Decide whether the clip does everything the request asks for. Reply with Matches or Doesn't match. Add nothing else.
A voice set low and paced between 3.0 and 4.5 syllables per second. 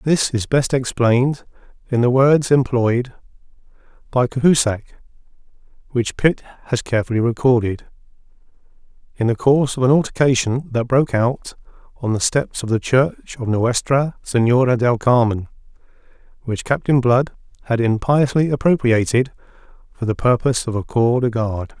Doesn't match